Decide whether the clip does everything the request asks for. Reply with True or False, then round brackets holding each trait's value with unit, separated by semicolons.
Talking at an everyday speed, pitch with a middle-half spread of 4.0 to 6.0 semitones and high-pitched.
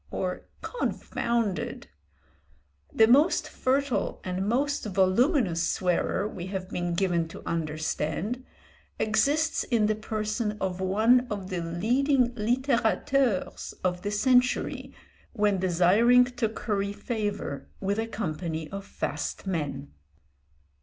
False (110 wpm; 4.8 semitones; 210 Hz)